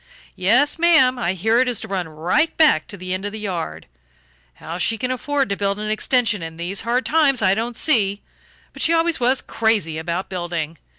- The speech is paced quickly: Yes, fast, 210 wpm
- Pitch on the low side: No, high, 215 Hz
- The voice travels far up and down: Yes, wide, 5.8 semitones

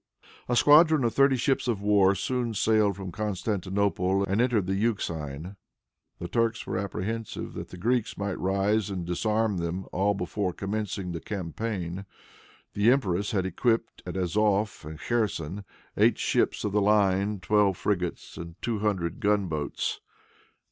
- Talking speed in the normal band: Yes, average, 150 wpm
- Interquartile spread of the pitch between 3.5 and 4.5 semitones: No, average, 2.9 semitones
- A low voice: Yes, low, 100 Hz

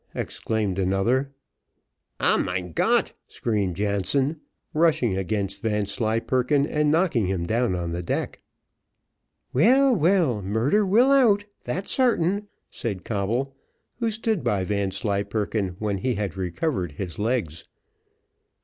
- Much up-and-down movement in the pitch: Yes, wide, 7.7 semitones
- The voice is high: No, low, 110 Hz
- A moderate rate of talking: No, slow, 115 wpm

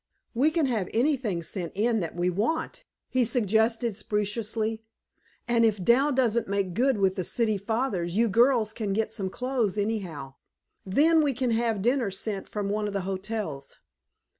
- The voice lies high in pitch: Yes, high, 220 Hz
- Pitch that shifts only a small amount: No, average, 3.5 semitones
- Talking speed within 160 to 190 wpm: Yes, average, 165 wpm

